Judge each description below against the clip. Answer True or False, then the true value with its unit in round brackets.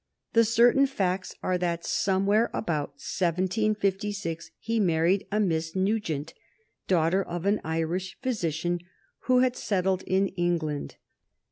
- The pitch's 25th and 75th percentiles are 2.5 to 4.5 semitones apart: True (3.8 semitones)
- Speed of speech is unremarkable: False (120 wpm)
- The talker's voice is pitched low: False (185 Hz)